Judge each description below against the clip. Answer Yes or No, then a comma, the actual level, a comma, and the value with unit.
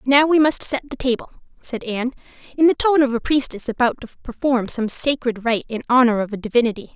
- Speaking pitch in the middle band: No, very high, 250 Hz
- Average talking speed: No, fast, 215 wpm